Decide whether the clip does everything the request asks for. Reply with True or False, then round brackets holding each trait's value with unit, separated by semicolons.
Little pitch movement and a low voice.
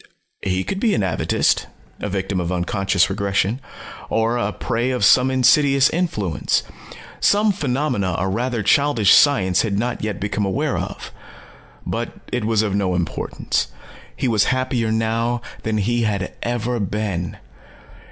False (4.2 semitones; 110 Hz)